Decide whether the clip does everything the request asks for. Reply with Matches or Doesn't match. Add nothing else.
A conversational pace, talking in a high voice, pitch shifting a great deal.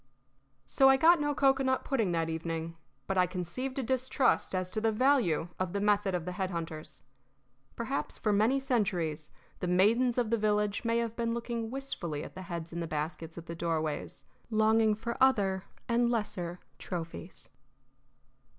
Matches